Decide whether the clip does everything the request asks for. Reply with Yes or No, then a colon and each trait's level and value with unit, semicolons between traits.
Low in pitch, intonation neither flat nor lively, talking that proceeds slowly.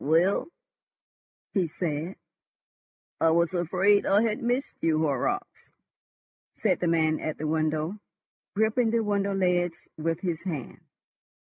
No: medium, 175 Hz; average, 4.1 semitones; slow, 125 wpm